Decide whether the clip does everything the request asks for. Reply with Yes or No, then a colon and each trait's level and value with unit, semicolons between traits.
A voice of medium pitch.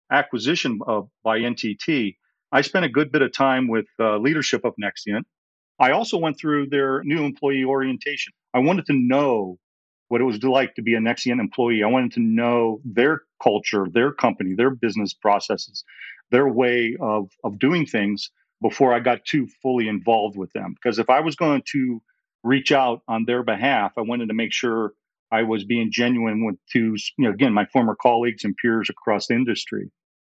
No: low, 120 Hz